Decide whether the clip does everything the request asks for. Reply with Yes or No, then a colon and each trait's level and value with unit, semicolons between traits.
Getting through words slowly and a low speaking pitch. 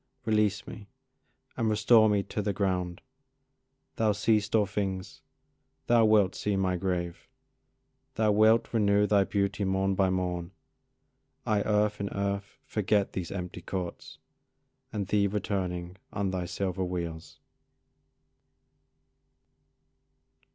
Yes: slow, 115 wpm; low, 100 Hz